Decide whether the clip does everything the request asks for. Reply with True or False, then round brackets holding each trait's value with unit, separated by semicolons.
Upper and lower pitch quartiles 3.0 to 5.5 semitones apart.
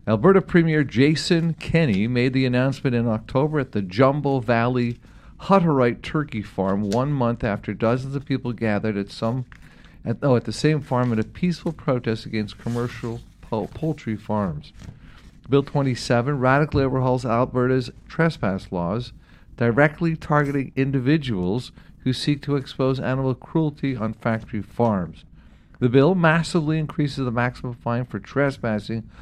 True (4.2 semitones)